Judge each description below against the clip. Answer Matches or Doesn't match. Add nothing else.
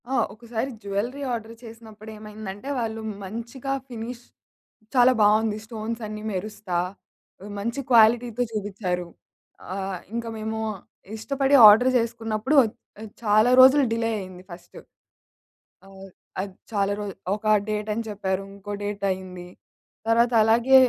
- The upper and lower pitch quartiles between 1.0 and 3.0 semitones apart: Matches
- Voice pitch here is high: Matches